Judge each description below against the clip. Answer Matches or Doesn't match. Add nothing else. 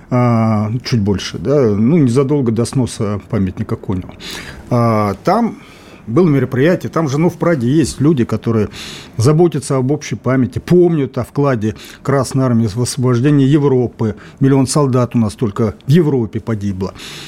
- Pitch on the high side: Doesn't match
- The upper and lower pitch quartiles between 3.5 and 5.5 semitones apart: Matches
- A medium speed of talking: Matches